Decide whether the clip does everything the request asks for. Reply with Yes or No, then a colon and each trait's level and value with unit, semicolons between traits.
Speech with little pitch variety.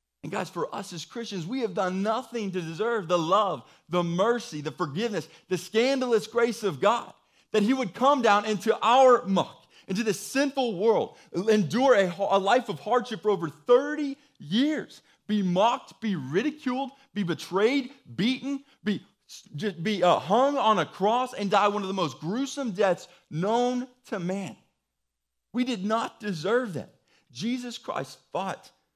No: average, 4.8 semitones